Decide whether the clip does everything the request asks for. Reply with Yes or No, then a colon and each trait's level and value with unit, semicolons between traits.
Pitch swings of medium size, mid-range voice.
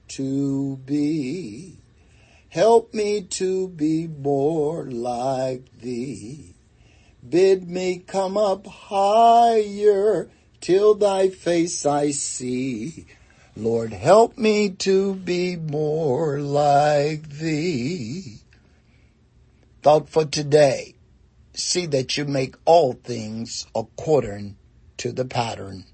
No: wide, 6.5 semitones; medium, 150 Hz